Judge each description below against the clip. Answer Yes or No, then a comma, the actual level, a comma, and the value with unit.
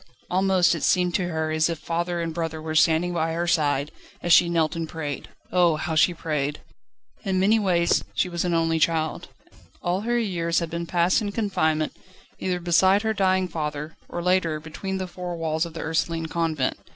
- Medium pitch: Yes, medium, 170 Hz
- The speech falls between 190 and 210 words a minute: Yes, average, 195 wpm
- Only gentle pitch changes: Yes, narrow, 2.2 semitones